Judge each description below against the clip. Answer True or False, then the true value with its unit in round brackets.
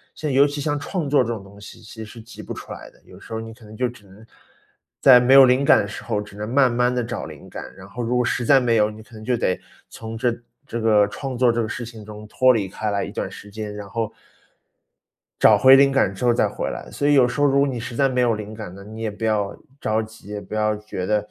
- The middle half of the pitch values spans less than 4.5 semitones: True (2.9 semitones)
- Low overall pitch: True (115 Hz)